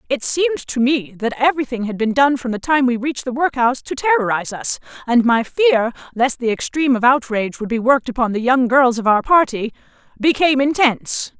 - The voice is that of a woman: Yes, female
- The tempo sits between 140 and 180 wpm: No, fast, 205 wpm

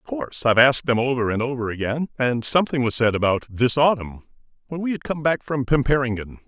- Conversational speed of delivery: No, fast, 215 wpm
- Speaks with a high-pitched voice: No, low, 130 Hz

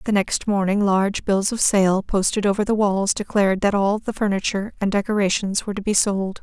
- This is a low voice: No, high, 200 Hz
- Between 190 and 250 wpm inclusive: Yes, fast, 205 wpm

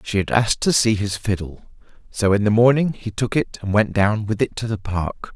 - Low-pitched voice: Yes, low, 110 Hz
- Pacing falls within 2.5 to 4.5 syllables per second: No, 5.2 syllables/s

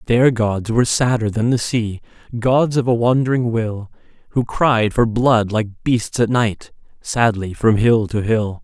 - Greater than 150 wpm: Yes, average, 175 wpm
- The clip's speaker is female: No, male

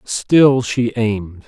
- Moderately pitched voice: No, low, 115 Hz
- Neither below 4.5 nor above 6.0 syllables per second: No, 3.0 syllables/s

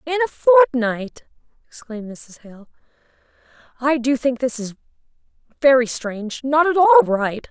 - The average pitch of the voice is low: No, very high, 265 Hz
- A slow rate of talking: Yes, slow, 130 wpm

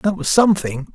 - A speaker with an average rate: Yes, average, 190 wpm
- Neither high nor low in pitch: Yes, medium, 180 Hz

